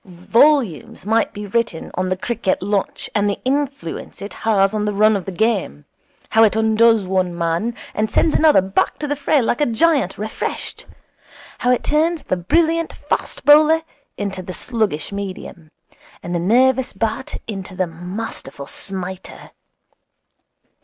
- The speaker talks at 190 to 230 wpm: No, average, 155 wpm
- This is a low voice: No, high, 210 Hz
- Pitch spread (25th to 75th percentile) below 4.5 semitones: No, average, 5.0 semitones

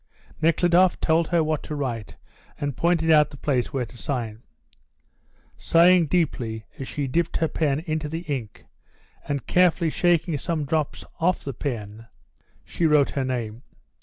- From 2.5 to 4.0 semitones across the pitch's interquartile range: No, average, 4.4 semitones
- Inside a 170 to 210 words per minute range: No, average, 155 wpm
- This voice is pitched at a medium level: Yes, medium, 150 Hz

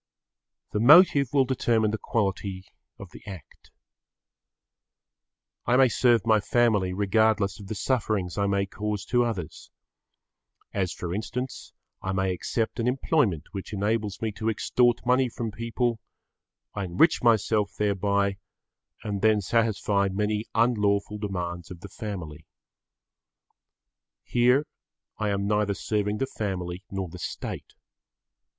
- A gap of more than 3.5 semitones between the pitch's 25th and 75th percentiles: No, average, 2.9 semitones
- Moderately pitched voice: No, low, 105 Hz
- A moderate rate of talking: No, slow, 130 wpm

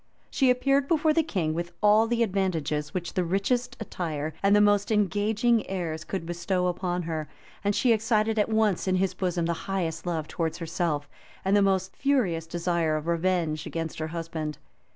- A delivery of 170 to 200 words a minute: Yes, average, 180 wpm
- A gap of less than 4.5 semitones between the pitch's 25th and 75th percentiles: Yes, average, 4.1 semitones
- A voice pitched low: No, medium, 185 Hz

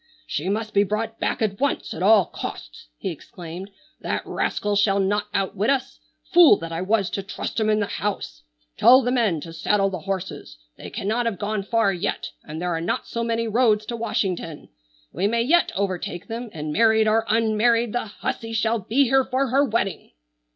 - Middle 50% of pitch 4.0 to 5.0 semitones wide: No, average, 3.3 semitones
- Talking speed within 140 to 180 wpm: No, average, 195 wpm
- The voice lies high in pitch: Yes, high, 210 Hz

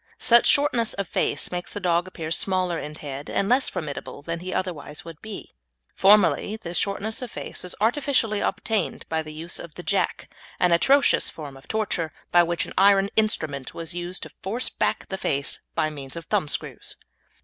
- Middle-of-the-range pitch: Yes, medium, 180 Hz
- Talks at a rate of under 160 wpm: No, average, 185 wpm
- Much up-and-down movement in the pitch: No, average, 4.7 semitones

